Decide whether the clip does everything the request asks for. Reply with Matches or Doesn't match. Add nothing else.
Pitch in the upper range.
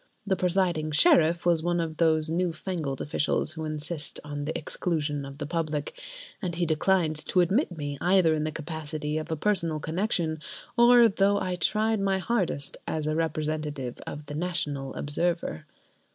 Doesn't match